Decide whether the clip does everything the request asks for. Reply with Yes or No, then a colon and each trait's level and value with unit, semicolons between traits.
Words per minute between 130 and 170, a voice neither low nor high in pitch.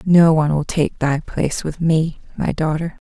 No: average, 195 wpm; medium, 160 Hz